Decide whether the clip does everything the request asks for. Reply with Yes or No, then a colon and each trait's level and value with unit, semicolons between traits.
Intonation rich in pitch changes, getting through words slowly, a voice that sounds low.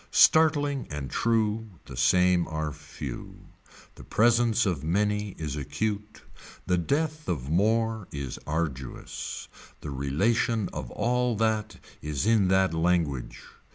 Yes: wide, 6.8 semitones; slow, 120 wpm; very low, 95 Hz